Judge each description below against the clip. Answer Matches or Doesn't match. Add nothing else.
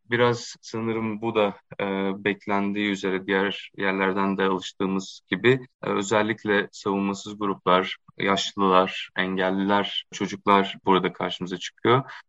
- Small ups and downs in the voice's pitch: Matches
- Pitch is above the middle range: Doesn't match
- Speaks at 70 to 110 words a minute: Matches